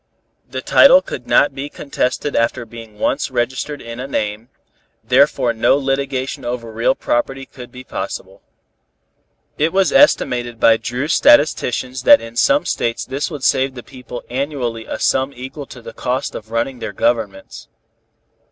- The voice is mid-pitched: No, low, 130 Hz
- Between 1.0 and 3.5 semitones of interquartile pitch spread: Yes, average, 2.9 semitones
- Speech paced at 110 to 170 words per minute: Yes, average, 155 wpm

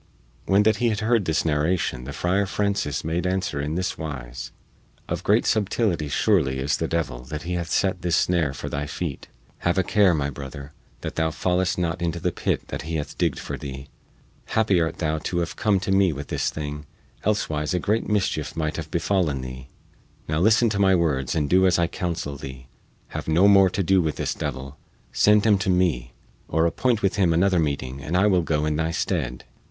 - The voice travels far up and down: No, average, 4.4 semitones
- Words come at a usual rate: No, fast, 210 wpm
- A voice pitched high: No, very low, 85 Hz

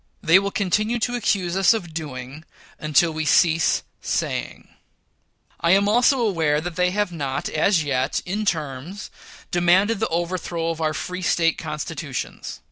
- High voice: No, medium, 170 Hz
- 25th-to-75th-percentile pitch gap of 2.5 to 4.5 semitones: Yes, average, 4.1 semitones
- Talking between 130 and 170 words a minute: Yes, average, 145 wpm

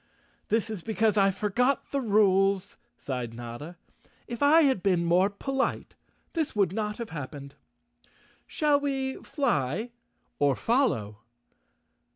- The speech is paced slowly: Yes, slow, 130 wpm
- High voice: Yes, high, 205 Hz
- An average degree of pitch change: No, wide, 7.1 semitones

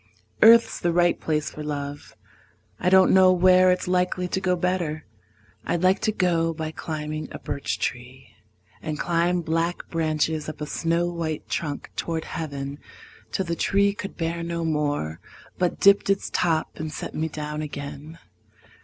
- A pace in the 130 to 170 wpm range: Yes, average, 160 wpm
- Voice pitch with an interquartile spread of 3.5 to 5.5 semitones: No, average, 3.0 semitones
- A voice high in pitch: No, medium, 165 Hz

